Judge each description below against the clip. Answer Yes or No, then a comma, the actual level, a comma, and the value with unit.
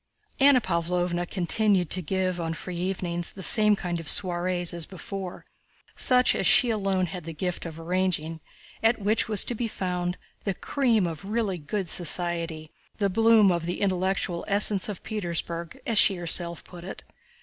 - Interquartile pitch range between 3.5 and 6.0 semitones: No, average, 2.9 semitones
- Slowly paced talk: No, average, 160 wpm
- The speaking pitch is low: No, medium, 185 Hz